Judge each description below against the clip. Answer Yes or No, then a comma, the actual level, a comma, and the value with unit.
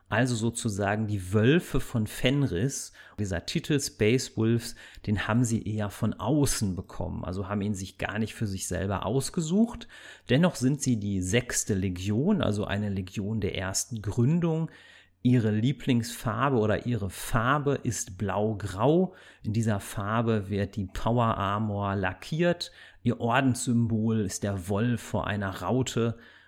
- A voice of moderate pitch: No, low, 110 Hz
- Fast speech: No, average, 140 wpm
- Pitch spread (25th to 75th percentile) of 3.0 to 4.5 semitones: Yes, average, 3.8 semitones